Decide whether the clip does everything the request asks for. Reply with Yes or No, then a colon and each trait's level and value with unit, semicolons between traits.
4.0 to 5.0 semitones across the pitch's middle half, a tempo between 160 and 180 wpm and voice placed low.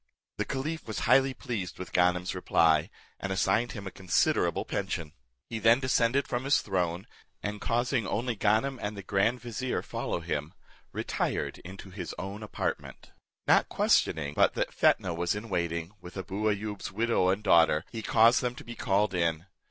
Yes: average, 4.7 semitones; average, 170 wpm; low, 100 Hz